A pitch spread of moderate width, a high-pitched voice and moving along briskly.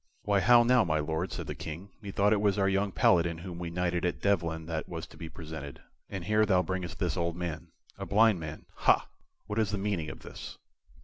No: average, 3.5 semitones; very low, 90 Hz; fast, 225 wpm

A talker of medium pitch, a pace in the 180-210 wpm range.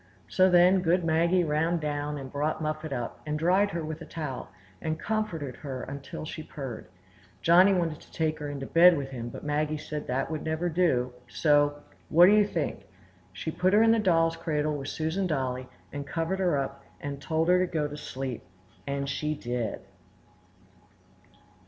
Yes: medium, 155 Hz; average, 185 wpm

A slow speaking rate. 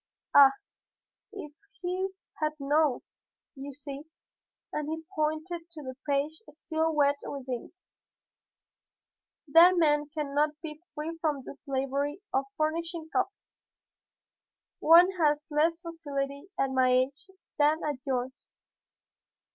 Yes: slow, 115 wpm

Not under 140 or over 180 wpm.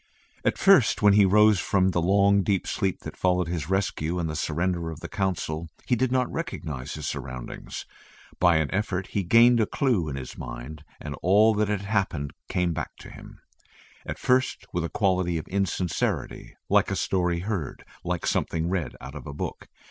No: average, 190 wpm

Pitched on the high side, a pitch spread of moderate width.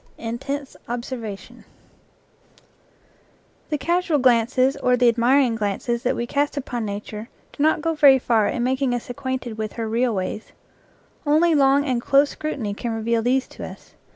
Yes: very high, 250 Hz; average, 3.5 semitones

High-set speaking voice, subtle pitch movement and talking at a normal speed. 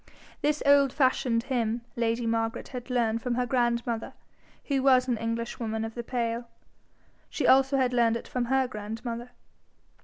Yes: high, 240 Hz; narrow, 2.0 semitones; average, 155 wpm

